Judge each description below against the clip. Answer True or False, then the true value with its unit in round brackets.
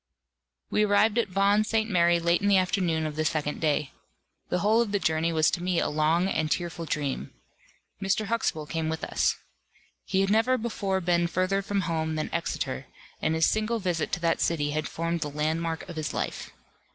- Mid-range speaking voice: True (170 Hz)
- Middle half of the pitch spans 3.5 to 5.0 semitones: True (3.9 semitones)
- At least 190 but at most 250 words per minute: True (200 wpm)